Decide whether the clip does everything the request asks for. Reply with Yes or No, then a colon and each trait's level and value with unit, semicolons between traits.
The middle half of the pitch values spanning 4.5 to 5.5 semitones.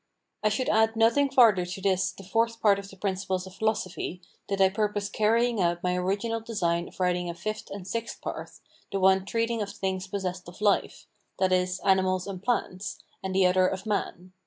No: average, 2.7 semitones